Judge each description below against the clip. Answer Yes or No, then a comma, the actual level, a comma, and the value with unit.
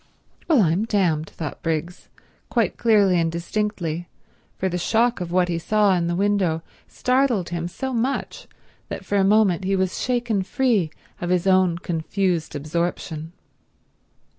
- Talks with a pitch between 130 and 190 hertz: Yes, medium, 185 Hz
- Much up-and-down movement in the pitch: No, average, 3.8 semitones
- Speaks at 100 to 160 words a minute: Yes, average, 150 wpm